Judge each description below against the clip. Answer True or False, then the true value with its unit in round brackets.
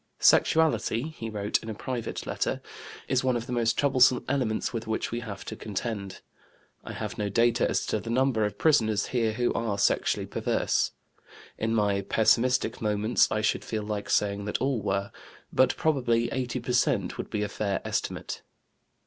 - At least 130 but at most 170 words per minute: False (180 wpm)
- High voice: False (115 Hz)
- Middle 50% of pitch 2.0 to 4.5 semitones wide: True (3.1 semitones)